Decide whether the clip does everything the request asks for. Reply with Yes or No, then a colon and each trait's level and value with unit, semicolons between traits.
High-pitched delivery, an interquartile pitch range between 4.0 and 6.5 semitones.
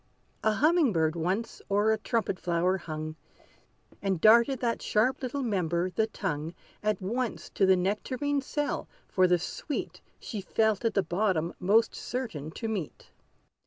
Yes: high, 205 Hz; average, 4.6 semitones